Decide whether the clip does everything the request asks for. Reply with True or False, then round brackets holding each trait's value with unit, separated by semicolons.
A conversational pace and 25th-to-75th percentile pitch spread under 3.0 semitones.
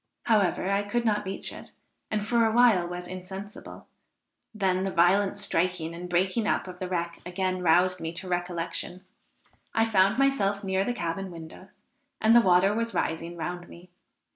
True (170 wpm; 2.6 semitones)